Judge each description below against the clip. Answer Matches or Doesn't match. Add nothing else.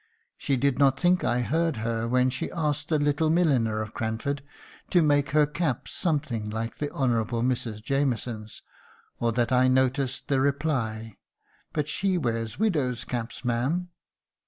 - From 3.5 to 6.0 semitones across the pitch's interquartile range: Matches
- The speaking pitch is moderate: Doesn't match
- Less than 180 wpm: Matches